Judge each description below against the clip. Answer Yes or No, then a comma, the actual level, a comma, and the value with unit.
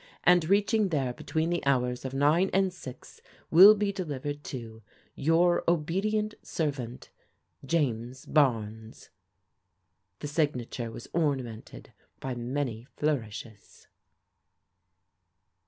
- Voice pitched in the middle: Yes, medium, 145 Hz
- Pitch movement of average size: No, wide, 5.8 semitones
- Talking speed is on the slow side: Yes, slow, 105 wpm